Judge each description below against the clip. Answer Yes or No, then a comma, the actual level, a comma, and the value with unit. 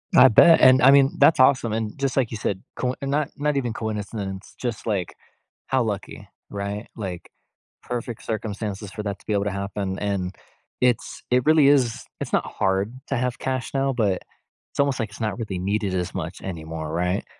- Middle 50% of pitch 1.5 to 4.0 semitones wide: No, average, 4.6 semitones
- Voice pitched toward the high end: No, low, 110 Hz